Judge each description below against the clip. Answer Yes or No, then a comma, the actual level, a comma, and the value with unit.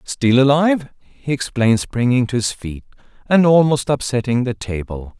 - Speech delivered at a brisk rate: No, average, 150 wpm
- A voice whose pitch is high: No, low, 125 Hz